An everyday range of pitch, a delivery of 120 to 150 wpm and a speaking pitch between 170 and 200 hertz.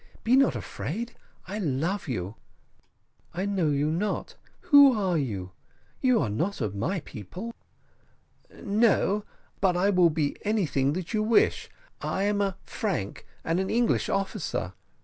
No: wide, 6.1 semitones; average, 145 wpm; high, 190 Hz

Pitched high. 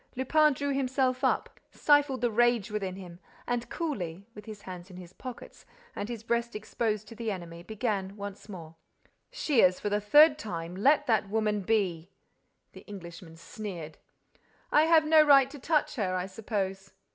Yes: high, 210 Hz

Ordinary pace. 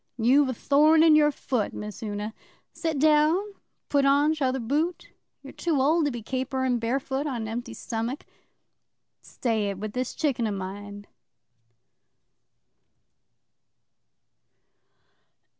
No: slow, 130 wpm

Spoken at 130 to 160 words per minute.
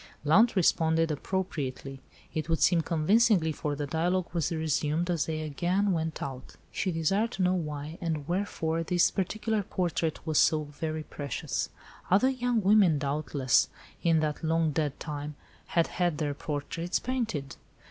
Yes: average, 150 wpm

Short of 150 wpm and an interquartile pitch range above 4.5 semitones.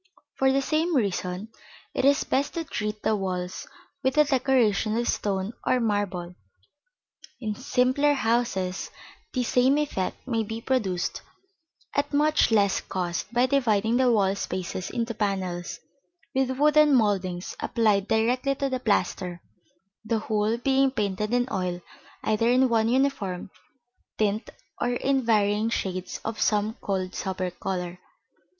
Yes: average, 140 wpm; average, 5.0 semitones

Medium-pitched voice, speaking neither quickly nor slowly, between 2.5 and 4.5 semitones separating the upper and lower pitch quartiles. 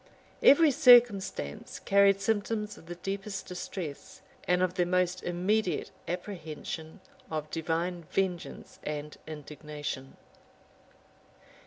No: medium, 180 Hz; slow, 100 wpm; average, 3.9 semitones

